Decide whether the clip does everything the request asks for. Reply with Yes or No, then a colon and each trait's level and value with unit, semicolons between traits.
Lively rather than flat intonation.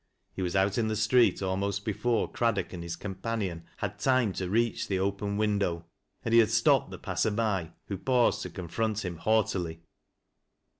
No: average, 3.0 semitones